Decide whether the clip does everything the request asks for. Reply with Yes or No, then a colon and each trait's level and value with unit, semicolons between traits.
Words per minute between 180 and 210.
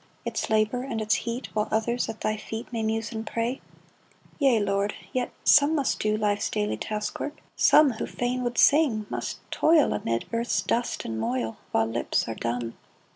Yes: average, 185 wpm